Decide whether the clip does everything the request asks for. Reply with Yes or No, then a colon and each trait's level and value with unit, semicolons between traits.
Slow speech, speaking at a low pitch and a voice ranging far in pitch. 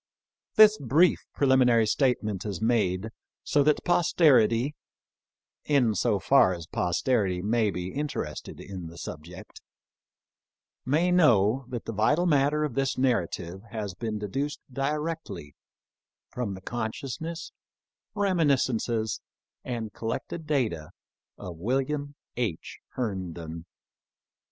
Yes: slow, 110 wpm; low, 120 Hz; wide, 6.6 semitones